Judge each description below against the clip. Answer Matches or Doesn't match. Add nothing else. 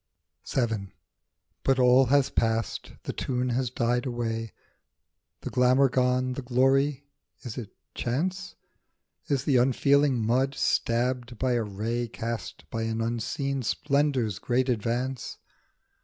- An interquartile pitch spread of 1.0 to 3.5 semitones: Matches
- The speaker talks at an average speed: Doesn't match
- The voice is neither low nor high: Doesn't match